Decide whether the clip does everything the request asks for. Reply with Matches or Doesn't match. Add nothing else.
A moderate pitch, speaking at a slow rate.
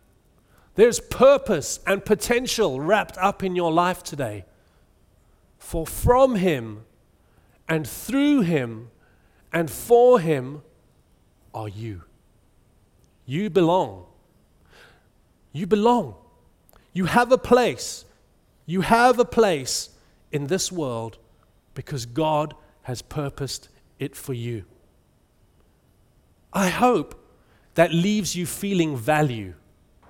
Matches